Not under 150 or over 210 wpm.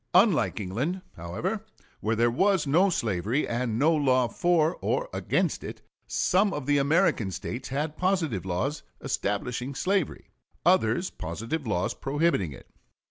No: slow, 135 wpm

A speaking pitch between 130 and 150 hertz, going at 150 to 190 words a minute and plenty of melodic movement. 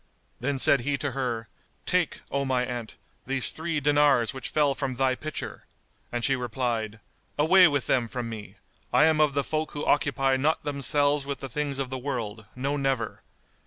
No: low, 135 Hz; average, 185 wpm; average, 2.8 semitones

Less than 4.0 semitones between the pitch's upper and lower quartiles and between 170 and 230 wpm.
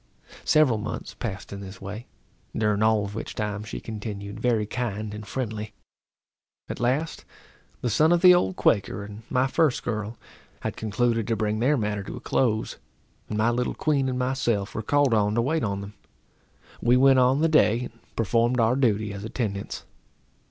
Yes: average, 3.2 semitones; average, 180 wpm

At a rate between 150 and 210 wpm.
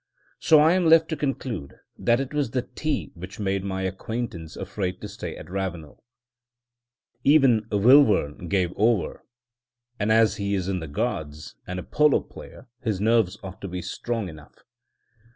Yes: average, 160 wpm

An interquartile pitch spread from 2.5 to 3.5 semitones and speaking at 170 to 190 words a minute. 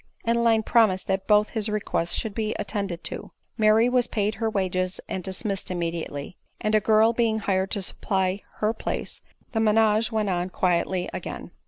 Yes: average, 2.9 semitones; average, 180 wpm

